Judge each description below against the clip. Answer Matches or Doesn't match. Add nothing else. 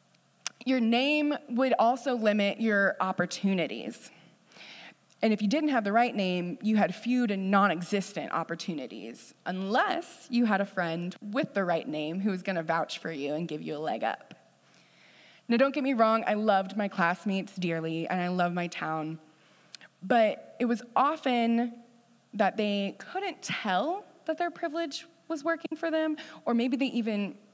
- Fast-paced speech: Doesn't match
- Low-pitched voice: Doesn't match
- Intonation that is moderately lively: Doesn't match